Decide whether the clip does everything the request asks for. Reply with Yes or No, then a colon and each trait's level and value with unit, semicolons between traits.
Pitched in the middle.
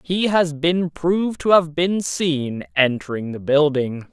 Yes: medium, 155 Hz